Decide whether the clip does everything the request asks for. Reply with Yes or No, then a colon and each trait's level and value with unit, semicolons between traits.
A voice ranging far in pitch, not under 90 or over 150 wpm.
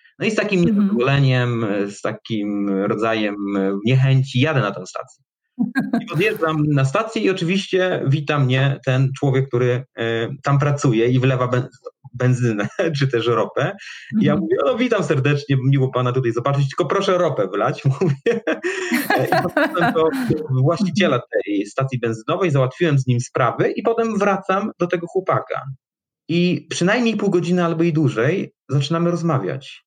Yes: wide, 6.0 semitones; average, 145 wpm